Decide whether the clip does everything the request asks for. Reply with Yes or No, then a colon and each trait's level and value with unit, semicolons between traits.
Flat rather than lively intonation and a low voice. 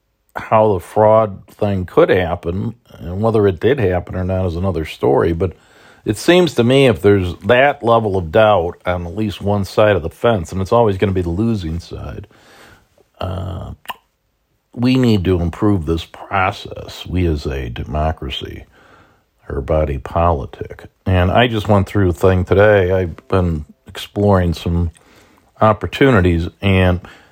No: average, 3.7 semitones; very low, 95 Hz